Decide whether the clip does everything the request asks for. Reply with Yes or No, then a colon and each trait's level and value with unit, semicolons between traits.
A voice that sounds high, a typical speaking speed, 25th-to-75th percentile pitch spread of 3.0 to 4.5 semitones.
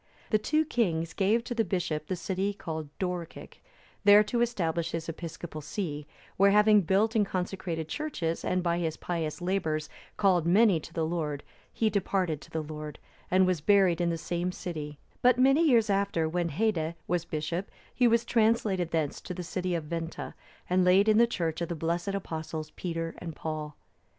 No: medium, 175 Hz; average, 185 wpm; average, 3.8 semitones